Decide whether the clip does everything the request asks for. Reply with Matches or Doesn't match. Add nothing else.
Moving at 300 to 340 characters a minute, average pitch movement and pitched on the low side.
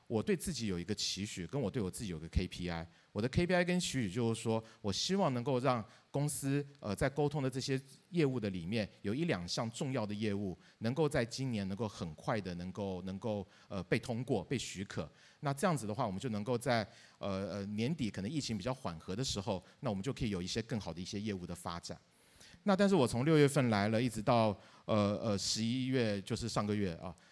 Matches